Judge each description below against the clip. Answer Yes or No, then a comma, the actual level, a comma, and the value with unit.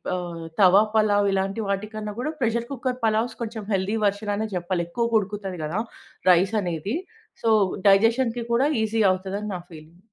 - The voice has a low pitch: No, high, 205 Hz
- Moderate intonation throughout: Yes, average, 3.2 semitones